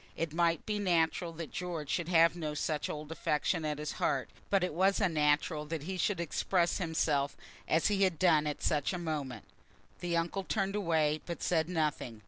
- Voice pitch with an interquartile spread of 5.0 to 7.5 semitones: No, average, 2.9 semitones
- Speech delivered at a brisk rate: No, average, 190 wpm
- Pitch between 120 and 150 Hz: No, medium, 165 Hz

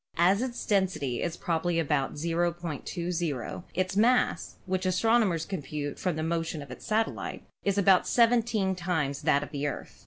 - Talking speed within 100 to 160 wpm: Yes, average, 155 wpm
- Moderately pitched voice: Yes, medium, 175 Hz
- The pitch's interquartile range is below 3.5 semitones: No, average, 3.9 semitones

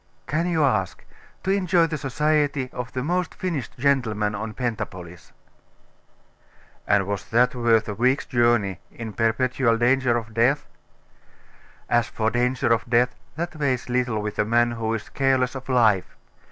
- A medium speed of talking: Yes, average, 155 wpm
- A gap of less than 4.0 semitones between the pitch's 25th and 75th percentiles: Yes, average, 3.3 semitones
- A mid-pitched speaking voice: No, low, 120 Hz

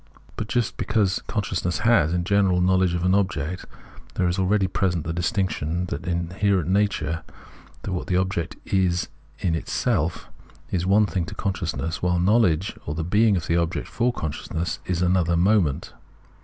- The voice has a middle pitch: No, very low, 90 Hz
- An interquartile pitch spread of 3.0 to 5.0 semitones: No, narrow, 2.6 semitones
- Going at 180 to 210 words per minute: No, average, 170 wpm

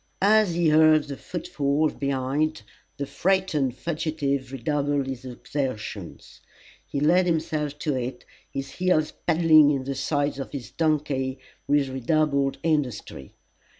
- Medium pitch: Yes, medium, 145 Hz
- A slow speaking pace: Yes, slow, 125 wpm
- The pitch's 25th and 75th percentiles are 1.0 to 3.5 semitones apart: Yes, narrow, 2.6 semitones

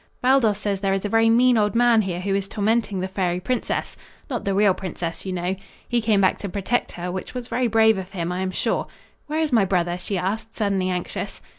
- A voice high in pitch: Yes, high, 200 Hz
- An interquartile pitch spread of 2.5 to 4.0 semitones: Yes, average, 3.3 semitones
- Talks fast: Yes, fast, 235 wpm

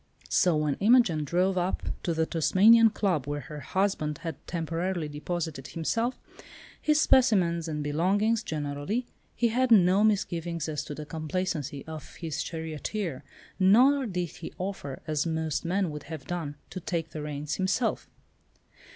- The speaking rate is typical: Yes, average, 150 wpm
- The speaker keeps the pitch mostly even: No, average, 4.3 semitones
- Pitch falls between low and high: Yes, medium, 170 Hz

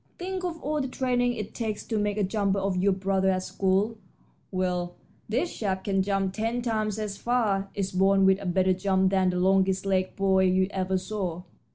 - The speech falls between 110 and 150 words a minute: No, average, 200 wpm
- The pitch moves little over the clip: Yes, narrow, 2.3 semitones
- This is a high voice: Yes, high, 195 Hz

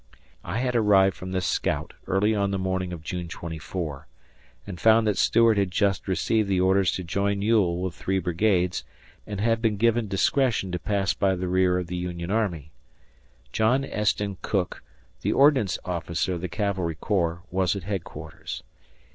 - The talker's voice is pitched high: No, very low, 95 Hz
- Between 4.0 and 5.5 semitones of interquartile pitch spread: No, average, 2.8 semitones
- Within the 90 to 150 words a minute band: No, average, 170 wpm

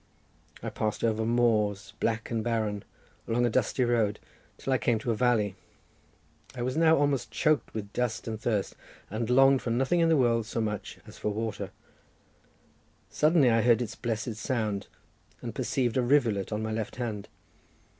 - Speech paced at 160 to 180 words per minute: Yes, average, 175 wpm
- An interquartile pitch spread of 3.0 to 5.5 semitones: No, narrow, 2.5 semitones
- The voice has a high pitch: No, low, 115 Hz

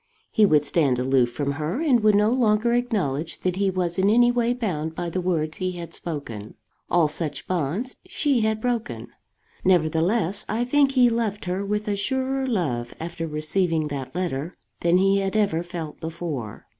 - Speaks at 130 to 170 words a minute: No, average, 180 wpm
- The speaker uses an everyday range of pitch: No, wide, 5.8 semitones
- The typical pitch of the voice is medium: Yes, medium, 180 Hz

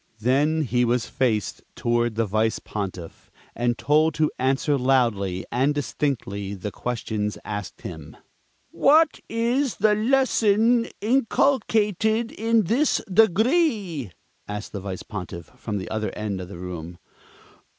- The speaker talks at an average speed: No, slow, 130 wpm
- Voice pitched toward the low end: Yes, low, 130 Hz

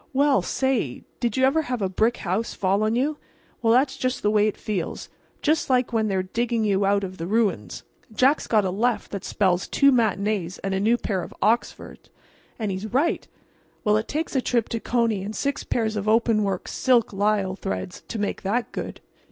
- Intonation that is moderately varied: Yes, average, 3.9 semitones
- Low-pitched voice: No, high, 215 Hz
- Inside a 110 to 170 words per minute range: No, average, 185 wpm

